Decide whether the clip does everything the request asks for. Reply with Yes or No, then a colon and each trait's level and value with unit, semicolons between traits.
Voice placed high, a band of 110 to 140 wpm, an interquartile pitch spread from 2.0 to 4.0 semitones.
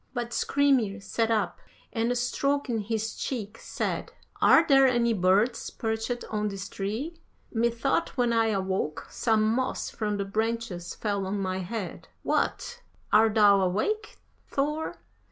Yes: high, 225 Hz; slow, 135 wpm; average, 3.3 semitones